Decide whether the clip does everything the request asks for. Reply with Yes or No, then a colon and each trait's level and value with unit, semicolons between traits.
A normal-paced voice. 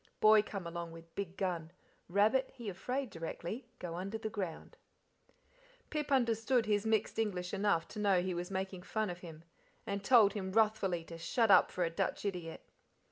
Yes: average, 180 wpm